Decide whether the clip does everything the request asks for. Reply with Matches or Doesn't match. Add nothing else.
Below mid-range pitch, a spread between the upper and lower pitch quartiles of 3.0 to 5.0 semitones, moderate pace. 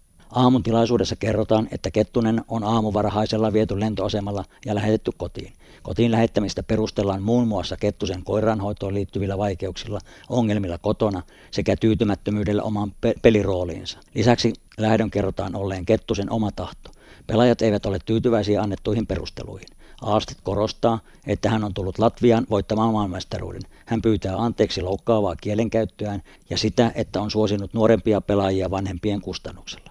Doesn't match